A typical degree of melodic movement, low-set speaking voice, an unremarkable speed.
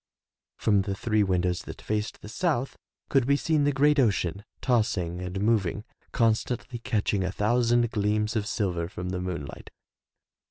Yes: average, 4.2 semitones; low, 105 Hz; average, 160 wpm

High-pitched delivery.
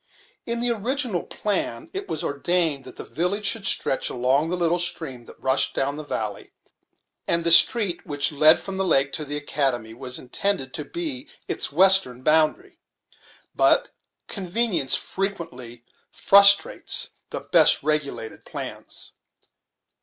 No: medium, 165 Hz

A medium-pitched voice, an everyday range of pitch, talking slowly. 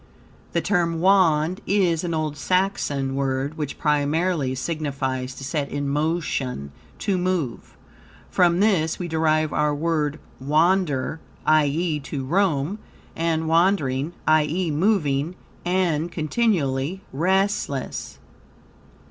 Yes: medium, 155 Hz; average, 3.9 semitones; slow, 105 wpm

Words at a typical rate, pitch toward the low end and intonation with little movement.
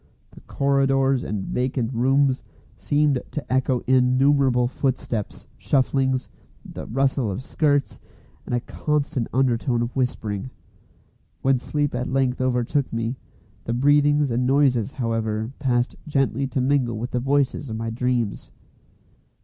No: slow, 130 wpm; low, 130 Hz; narrow, 2.3 semitones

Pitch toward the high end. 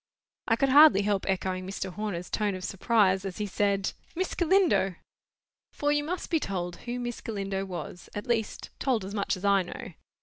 Yes: high, 200 Hz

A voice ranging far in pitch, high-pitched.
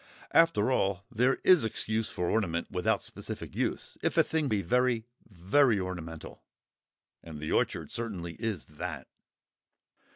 No: wide, 6.0 semitones; low, 105 Hz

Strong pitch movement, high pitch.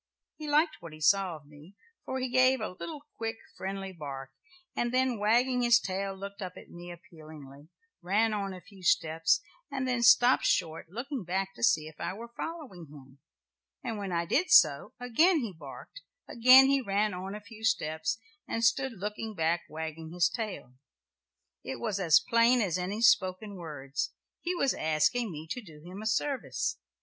Yes: wide, 6.5 semitones; high, 195 Hz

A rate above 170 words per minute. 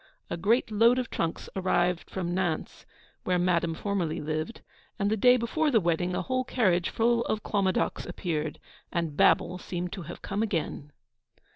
No: average, 165 wpm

